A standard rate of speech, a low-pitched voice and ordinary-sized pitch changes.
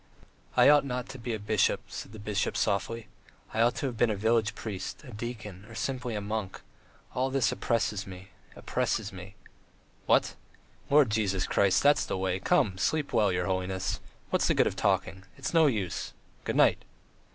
Yes: average, 185 wpm; low, 110 Hz; average, 4.1 semitones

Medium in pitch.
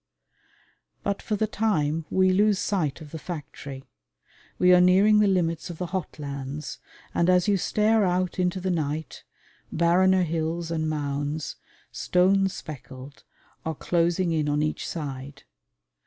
Yes: medium, 170 Hz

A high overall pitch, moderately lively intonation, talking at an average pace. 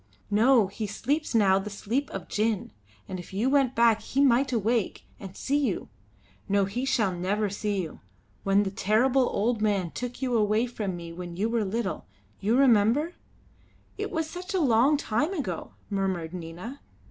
Yes: high, 220 Hz; average, 4.8 semitones; average, 180 wpm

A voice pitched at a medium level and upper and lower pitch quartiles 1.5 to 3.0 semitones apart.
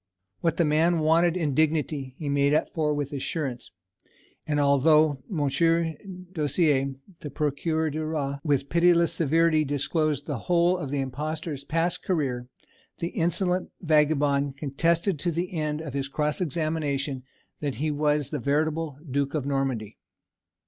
Yes: medium, 150 Hz; narrow, 2.6 semitones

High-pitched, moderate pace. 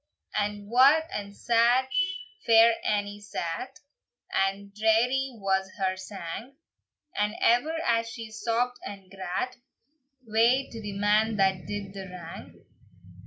No: high, 210 Hz; slow, 120 wpm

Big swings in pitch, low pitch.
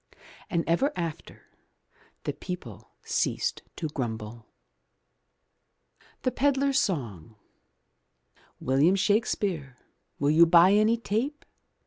No: wide, 8.0 semitones; medium, 170 Hz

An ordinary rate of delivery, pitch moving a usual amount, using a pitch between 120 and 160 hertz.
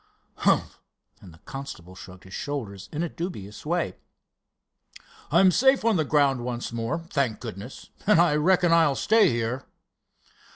No: average, 150 wpm; wide, 6.9 semitones; medium, 140 Hz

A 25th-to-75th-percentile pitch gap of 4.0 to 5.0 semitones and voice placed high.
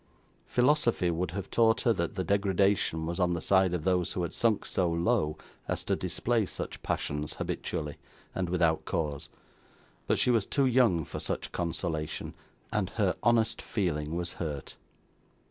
No: average, 4.4 semitones; very low, 90 Hz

